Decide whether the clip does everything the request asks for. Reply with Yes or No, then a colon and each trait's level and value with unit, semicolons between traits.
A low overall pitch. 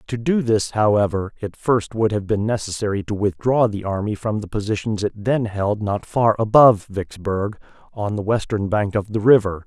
Yes: low, 105 Hz